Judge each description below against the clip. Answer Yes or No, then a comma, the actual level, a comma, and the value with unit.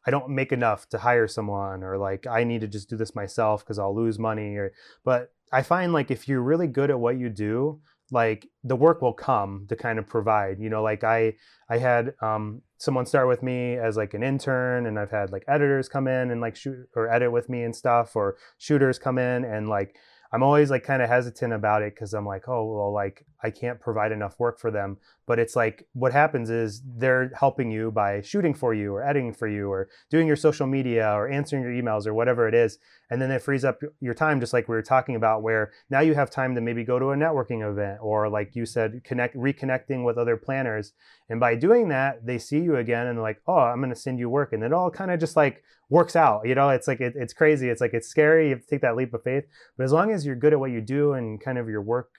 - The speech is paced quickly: Yes, fast, 260 wpm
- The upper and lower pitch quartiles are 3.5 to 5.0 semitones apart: Yes, average, 3.8 semitones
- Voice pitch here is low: Yes, low, 120 Hz